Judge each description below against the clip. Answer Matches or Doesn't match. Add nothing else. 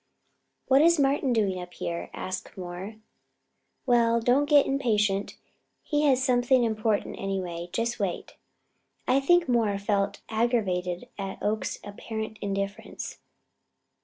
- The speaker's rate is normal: Doesn't match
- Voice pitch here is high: Matches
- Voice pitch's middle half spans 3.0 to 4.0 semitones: Doesn't match